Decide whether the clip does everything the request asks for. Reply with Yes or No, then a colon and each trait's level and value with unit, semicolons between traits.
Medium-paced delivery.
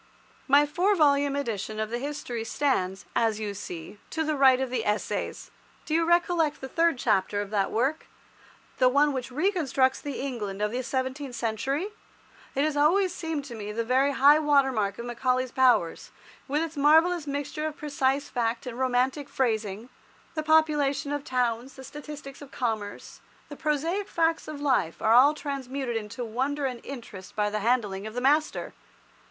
Yes: average, 175 wpm